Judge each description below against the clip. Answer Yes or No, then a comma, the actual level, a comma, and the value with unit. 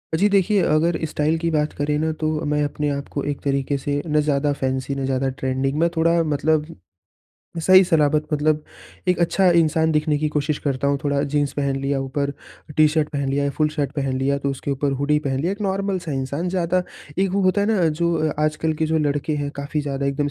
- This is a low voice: No, medium, 150 Hz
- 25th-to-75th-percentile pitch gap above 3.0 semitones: No, narrow, 2.5 semitones